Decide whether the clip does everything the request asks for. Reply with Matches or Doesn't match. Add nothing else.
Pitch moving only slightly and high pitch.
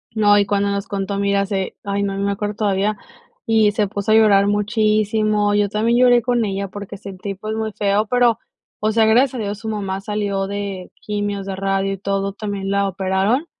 Matches